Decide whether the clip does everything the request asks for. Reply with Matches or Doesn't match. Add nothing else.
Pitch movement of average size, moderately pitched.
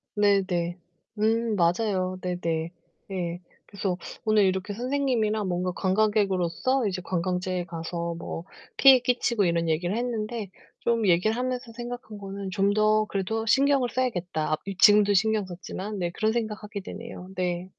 Doesn't match